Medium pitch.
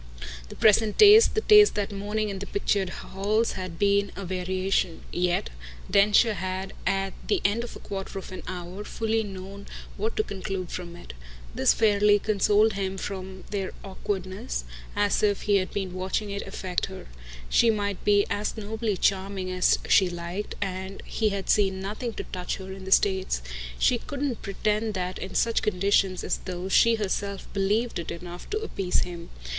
No: high, 195 Hz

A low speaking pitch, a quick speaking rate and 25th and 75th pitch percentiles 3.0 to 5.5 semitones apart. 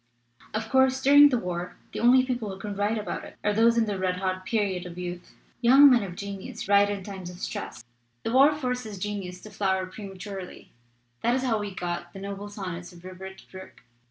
No: high, 200 Hz; fast, 215 wpm; average, 3.7 semitones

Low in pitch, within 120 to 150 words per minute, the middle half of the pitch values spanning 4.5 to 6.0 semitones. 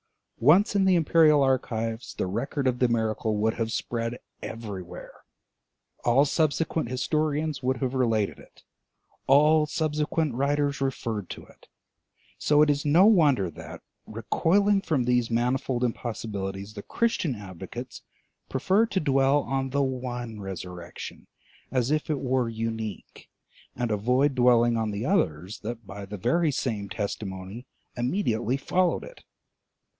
Yes: low, 125 Hz; slow, 135 wpm; average, 4.9 semitones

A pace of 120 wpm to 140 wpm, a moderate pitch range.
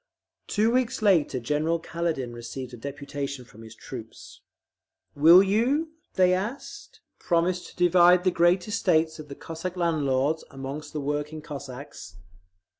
Yes: slow, 135 wpm; average, 4.6 semitones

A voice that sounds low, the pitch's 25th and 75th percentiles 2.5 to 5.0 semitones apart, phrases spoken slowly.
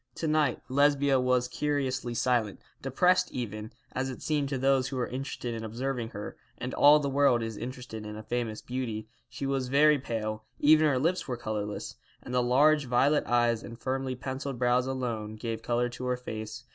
No: low, 125 Hz; average, 2.8 semitones; average, 190 wpm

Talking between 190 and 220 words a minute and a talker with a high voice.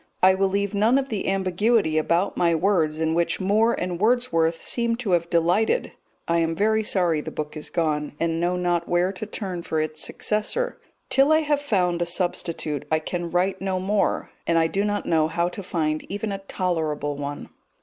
No: average, 200 wpm; medium, 180 Hz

